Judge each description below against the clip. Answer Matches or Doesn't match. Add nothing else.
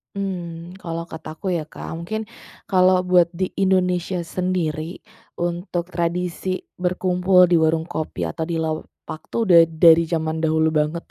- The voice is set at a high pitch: Doesn't match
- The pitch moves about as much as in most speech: Doesn't match